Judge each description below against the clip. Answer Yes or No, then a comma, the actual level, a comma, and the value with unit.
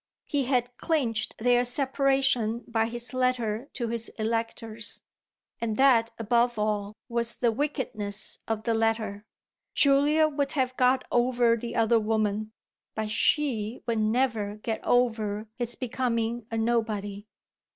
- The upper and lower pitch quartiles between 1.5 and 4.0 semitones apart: Yes, narrow, 2.4 semitones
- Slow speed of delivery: Yes, slow, 130 wpm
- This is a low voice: No, high, 235 Hz